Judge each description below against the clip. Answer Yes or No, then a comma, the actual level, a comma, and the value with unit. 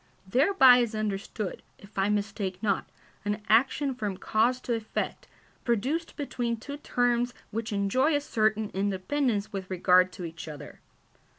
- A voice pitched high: Yes, high, 215 Hz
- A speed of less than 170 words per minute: Yes, average, 140 wpm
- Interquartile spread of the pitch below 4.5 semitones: Yes, average, 3.9 semitones